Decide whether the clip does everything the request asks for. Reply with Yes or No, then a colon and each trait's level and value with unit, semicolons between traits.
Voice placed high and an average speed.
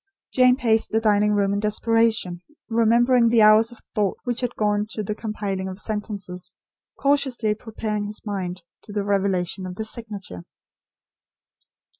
Yes: high, 210 Hz; average, 150 wpm